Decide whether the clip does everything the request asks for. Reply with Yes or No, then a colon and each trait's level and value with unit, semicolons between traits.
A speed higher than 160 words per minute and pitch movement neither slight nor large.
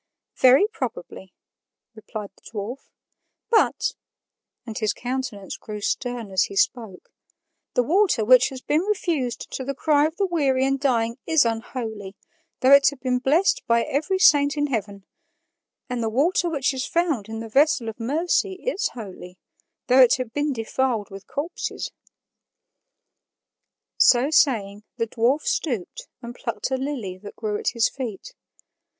No: average, 155 wpm; average, 4.7 semitones